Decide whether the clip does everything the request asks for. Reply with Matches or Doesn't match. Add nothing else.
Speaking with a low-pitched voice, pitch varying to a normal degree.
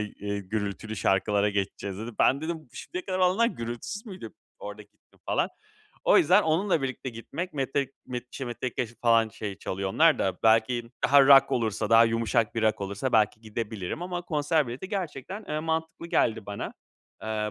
Doesn't match